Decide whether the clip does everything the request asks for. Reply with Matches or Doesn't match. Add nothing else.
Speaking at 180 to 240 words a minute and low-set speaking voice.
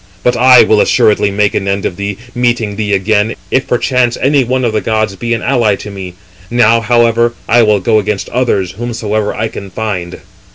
Matches